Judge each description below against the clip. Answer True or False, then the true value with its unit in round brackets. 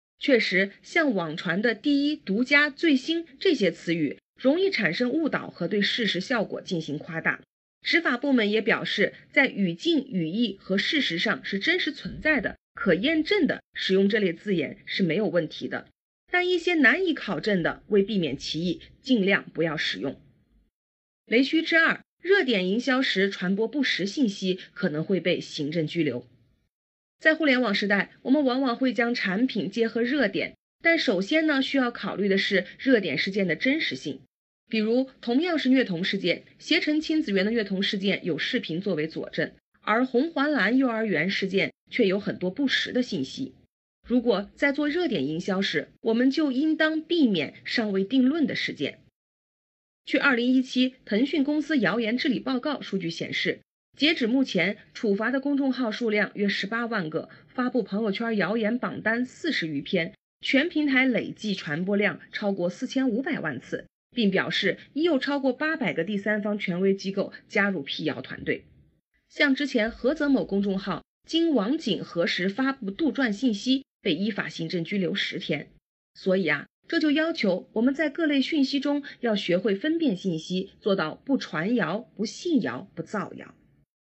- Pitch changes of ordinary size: False (6.2 semitones)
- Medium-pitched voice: False (225 Hz)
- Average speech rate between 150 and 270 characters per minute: True (260 characters per minute)